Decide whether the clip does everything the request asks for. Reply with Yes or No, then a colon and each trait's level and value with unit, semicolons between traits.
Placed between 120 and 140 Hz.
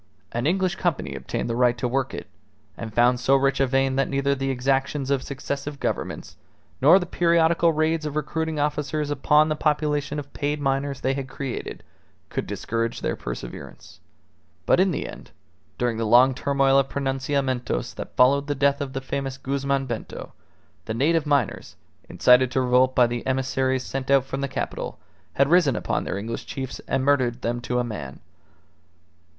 Yes: low, 135 Hz